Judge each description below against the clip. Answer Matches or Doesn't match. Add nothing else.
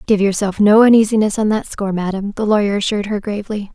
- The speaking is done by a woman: Matches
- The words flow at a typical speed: Doesn't match